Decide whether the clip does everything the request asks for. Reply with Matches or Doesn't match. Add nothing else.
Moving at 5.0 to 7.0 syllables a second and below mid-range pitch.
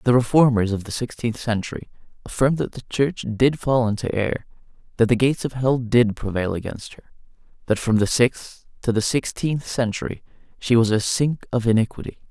Matches